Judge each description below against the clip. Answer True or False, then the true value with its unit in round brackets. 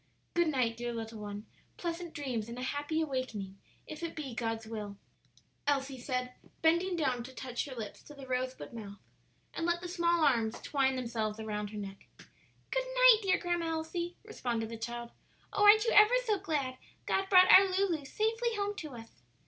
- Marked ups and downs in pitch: True (7.0 semitones)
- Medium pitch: False (270 Hz)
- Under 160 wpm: False (185 wpm)